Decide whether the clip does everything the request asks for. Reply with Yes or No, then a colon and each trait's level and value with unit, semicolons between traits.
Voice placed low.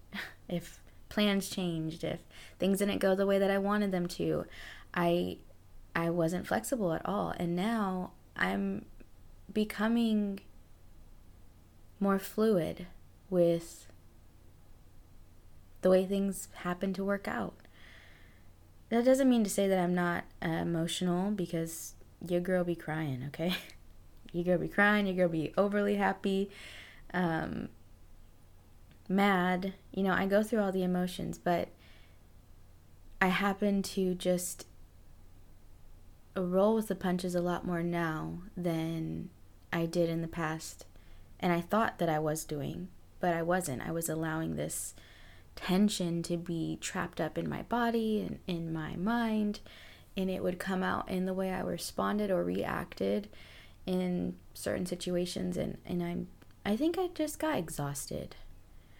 No: medium, 175 Hz